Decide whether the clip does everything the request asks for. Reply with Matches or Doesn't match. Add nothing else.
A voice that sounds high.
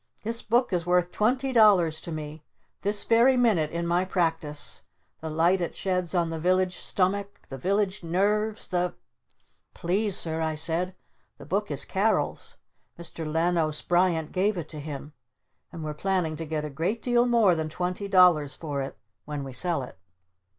Doesn't match